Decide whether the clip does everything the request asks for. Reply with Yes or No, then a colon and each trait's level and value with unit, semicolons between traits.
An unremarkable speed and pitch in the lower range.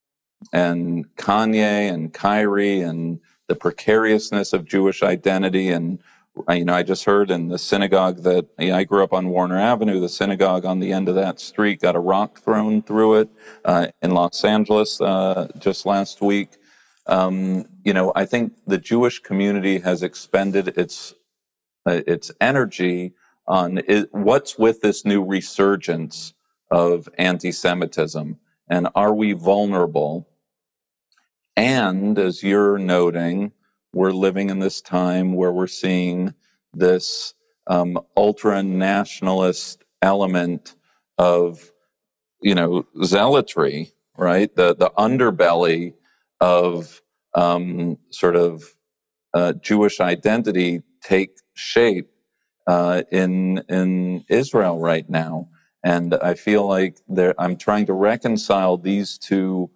No: slow, 130 wpm; very low, 95 Hz